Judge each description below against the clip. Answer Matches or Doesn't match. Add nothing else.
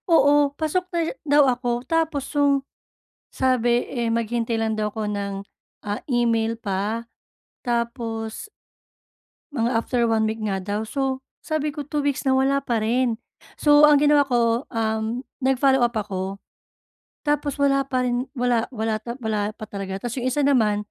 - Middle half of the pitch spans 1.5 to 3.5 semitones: Doesn't match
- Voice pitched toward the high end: Matches